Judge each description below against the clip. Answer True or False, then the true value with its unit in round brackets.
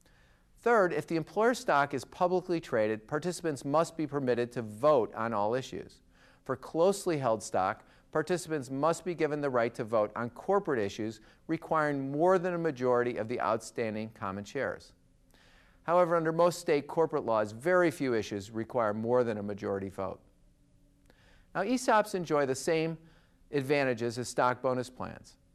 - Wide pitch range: True (6.3 semitones)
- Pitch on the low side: False (145 Hz)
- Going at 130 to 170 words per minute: True (155 wpm)